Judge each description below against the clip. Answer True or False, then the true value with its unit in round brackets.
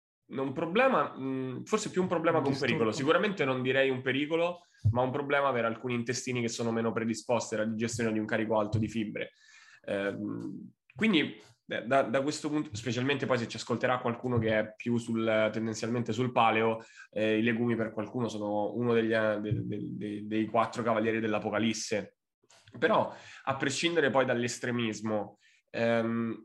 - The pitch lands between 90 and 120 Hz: True (115 Hz)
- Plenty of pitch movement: False (3.1 semitones)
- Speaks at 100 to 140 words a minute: False (155 wpm)